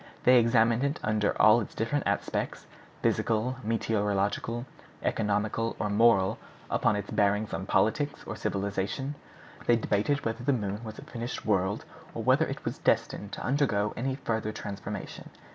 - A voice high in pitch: No, low, 110 Hz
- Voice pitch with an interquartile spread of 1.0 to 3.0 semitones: Yes, narrow, 2.6 semitones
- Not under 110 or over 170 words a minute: Yes, average, 155 wpm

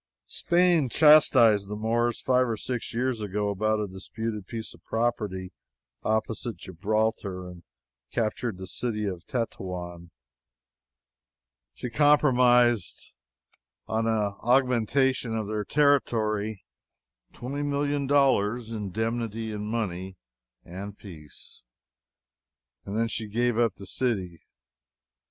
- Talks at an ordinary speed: No, slow, 110 wpm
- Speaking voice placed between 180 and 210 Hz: No, low, 110 Hz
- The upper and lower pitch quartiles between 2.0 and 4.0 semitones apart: Yes, average, 3.3 semitones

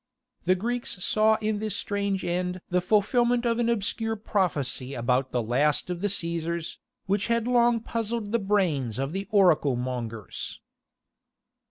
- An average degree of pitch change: No, wide, 6.5 semitones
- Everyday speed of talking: Yes, average, 150 wpm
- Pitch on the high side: Yes, high, 195 Hz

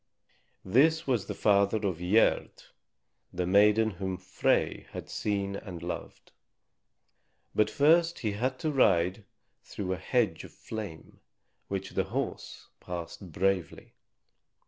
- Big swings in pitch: No, average, 3.4 semitones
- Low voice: Yes, low, 100 Hz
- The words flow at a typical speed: No, slow, 125 wpm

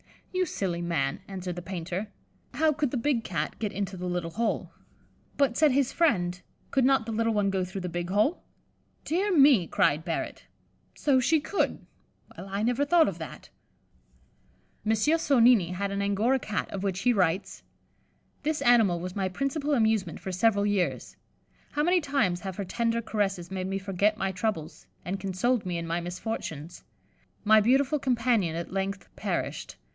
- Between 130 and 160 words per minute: No, average, 170 wpm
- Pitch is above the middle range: Yes, high, 205 Hz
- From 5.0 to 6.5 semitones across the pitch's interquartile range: Yes, wide, 5.6 semitones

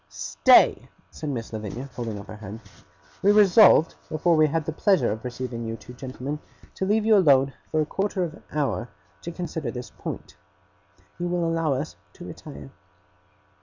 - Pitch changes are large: Yes, wide, 6.6 semitones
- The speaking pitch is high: No, medium, 145 Hz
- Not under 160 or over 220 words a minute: Yes, average, 175 wpm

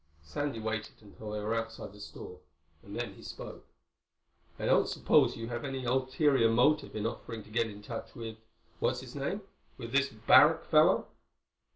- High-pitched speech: No, low, 115 Hz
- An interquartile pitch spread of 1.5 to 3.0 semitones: No, average, 3.5 semitones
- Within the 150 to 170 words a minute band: Yes, average, 165 wpm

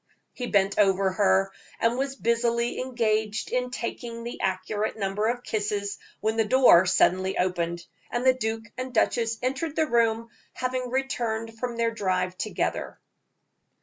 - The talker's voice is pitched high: Yes, high, 225 Hz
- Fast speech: No, average, 150 wpm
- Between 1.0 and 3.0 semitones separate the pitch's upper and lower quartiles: No, average, 3.6 semitones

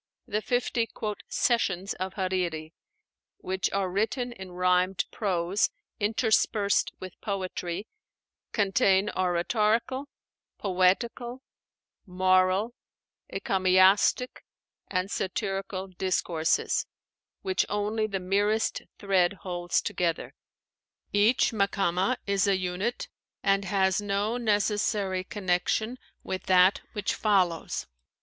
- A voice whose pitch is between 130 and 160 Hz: No, high, 195 Hz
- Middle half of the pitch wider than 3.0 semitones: No, narrow, 2.4 semitones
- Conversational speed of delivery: No, slow, 90 wpm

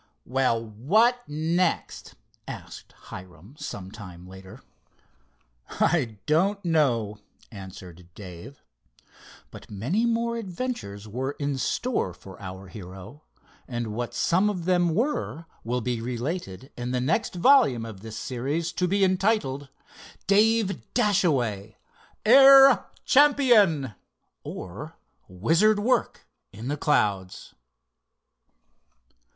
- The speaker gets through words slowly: Yes, slow, 105 wpm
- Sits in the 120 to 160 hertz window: Yes, medium, 140 Hz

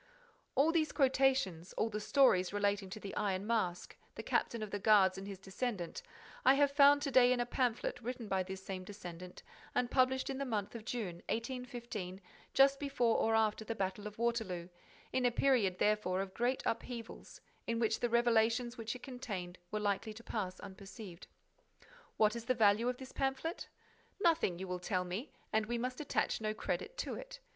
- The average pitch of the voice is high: Yes, high, 225 Hz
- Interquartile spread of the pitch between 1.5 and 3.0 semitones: No, average, 4.4 semitones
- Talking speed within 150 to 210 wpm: Yes, average, 190 wpm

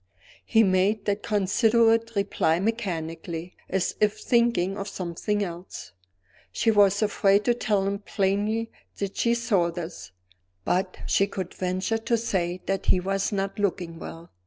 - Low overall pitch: No, high, 195 Hz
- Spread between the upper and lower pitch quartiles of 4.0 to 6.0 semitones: No, average, 2.9 semitones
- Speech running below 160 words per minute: Yes, average, 145 wpm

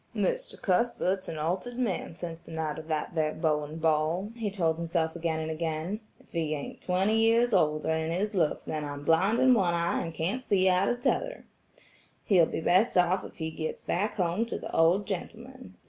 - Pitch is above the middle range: No, medium, 175 Hz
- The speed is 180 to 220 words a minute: Yes, average, 200 wpm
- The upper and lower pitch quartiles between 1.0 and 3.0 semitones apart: No, average, 4.4 semitones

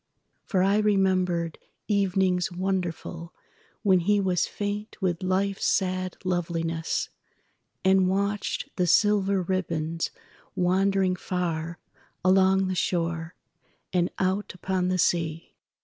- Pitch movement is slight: Yes, narrow, 1.8 semitones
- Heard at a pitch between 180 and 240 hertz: Yes, medium, 185 Hz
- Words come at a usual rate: No, slow, 95 wpm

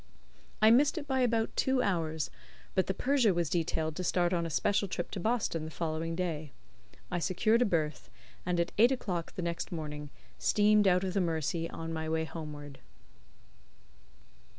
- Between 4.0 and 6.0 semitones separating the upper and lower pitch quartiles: Yes, average, 4.4 semitones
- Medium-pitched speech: Yes, medium, 175 Hz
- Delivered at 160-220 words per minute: Yes, average, 180 wpm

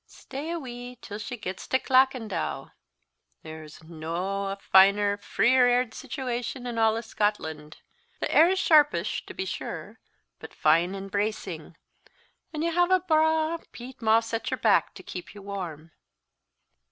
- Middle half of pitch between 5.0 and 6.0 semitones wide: Yes, wide, 5.4 semitones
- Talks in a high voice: Yes, high, 225 Hz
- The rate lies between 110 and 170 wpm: Yes, average, 150 wpm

